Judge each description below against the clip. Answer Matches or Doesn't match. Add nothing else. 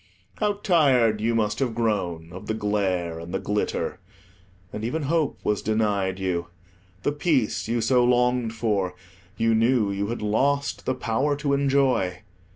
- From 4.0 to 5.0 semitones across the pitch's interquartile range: Matches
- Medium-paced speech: Matches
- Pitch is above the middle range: Doesn't match